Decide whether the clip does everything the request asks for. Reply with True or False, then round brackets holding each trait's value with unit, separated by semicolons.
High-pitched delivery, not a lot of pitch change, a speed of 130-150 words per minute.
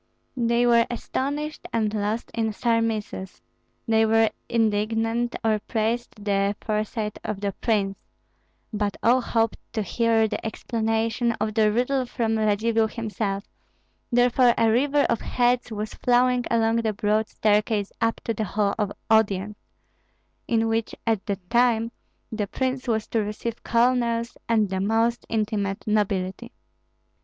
True (225 Hz; 1.9 semitones; 140 wpm)